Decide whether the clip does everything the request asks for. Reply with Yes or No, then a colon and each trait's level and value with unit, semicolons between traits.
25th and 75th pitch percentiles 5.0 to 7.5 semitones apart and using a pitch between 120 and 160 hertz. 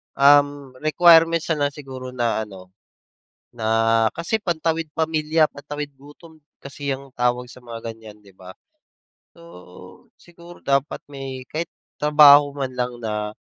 No: average, 4.2 semitones; medium, 140 Hz